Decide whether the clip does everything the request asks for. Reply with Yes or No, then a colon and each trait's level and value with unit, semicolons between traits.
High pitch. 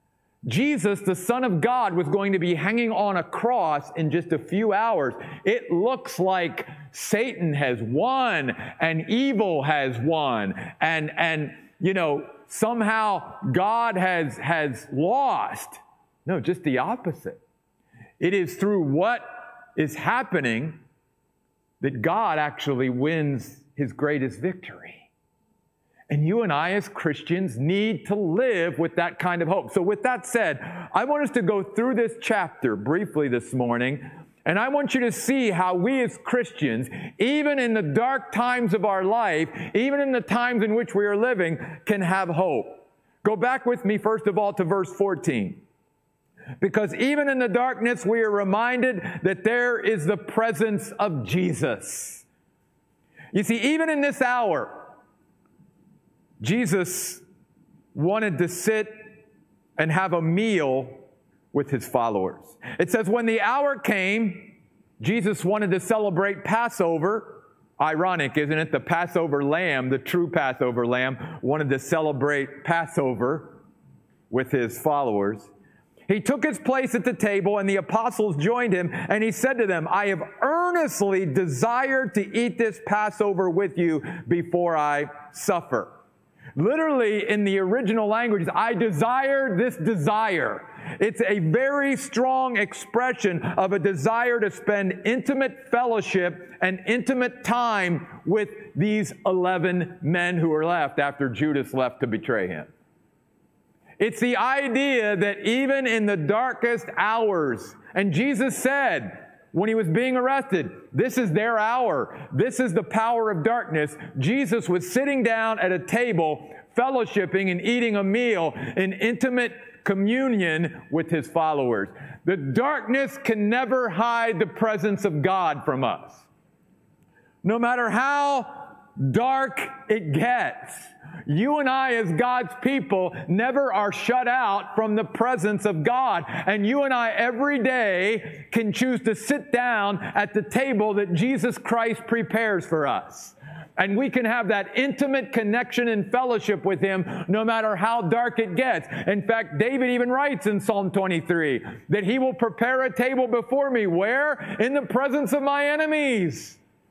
Yes: high, 205 Hz